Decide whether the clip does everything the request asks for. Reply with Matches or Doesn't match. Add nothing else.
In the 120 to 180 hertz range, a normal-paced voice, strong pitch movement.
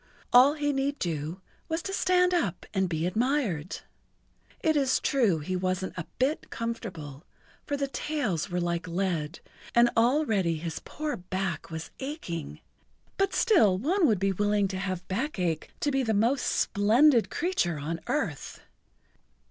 Doesn't match